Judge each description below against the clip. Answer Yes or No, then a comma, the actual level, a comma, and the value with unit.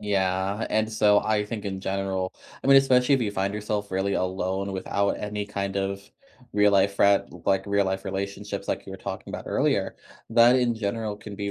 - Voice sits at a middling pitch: No, low, 100 Hz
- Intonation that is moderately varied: No, narrow, 1.5 semitones